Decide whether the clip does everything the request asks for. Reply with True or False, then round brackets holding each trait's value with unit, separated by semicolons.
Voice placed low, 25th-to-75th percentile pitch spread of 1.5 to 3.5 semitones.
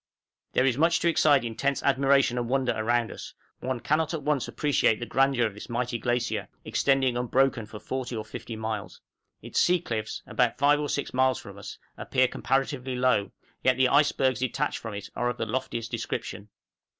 True (130 Hz; 2.7 semitones)